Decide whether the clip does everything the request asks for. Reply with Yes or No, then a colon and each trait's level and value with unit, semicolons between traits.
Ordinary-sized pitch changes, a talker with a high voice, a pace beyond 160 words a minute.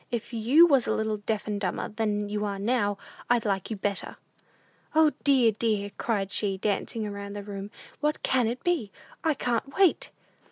Yes: average, 3.4 semitones; high, 215 Hz; average, 185 wpm